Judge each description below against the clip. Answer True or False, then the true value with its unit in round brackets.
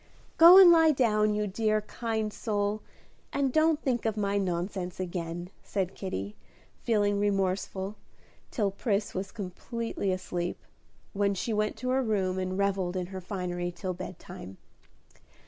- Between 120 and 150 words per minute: True (145 wpm)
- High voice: True (200 Hz)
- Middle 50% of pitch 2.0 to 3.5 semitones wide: True (2.9 semitones)